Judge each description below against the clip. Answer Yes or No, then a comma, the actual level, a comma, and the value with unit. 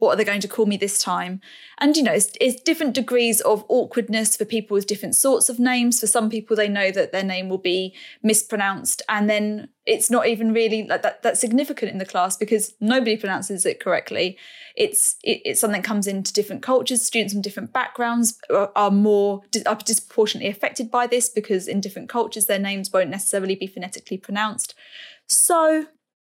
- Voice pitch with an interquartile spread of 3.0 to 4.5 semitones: Yes, average, 3.4 semitones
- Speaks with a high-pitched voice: Yes, high, 220 Hz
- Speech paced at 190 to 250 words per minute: Yes, average, 200 wpm